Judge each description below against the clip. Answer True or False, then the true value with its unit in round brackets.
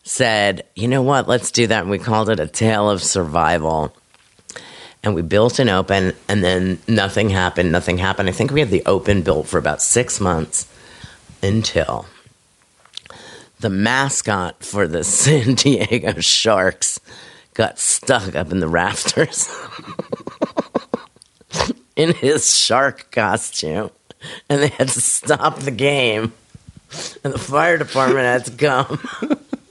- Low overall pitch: True (115 Hz)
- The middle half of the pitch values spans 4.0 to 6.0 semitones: True (5.6 semitones)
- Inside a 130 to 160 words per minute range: True (140 wpm)